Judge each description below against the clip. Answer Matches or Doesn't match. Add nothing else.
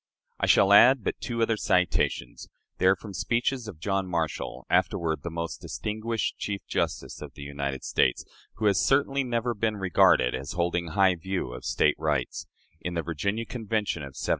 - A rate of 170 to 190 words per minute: Matches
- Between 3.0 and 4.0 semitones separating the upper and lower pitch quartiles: Doesn't match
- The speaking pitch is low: Matches